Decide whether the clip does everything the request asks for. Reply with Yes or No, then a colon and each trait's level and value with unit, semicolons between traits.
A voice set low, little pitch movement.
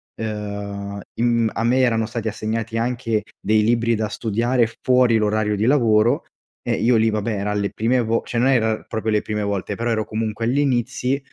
Yes: low, 110 Hz; narrow, 1.9 semitones